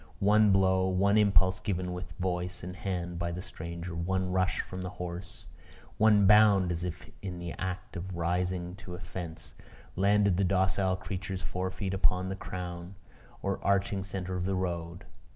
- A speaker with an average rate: Yes, average, 170 wpm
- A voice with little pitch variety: Yes, narrow, 1.5 semitones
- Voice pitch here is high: No, very low, 95 Hz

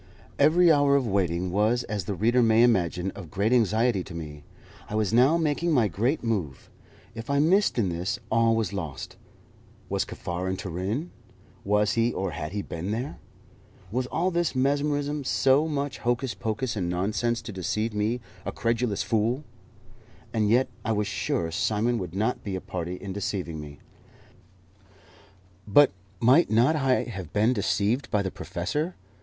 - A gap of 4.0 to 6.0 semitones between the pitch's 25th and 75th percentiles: Yes, average, 5.0 semitones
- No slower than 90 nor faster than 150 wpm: No, average, 165 wpm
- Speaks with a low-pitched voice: Yes, low, 110 Hz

